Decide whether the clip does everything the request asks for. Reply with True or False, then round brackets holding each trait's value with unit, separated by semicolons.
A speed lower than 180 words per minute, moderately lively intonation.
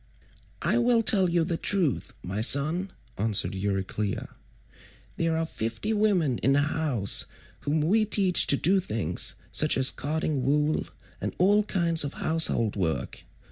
False (150 wpm; 7.9 semitones)